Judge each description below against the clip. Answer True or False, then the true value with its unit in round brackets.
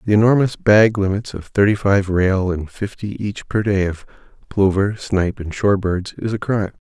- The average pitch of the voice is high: False (100 Hz)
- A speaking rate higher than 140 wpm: True (190 wpm)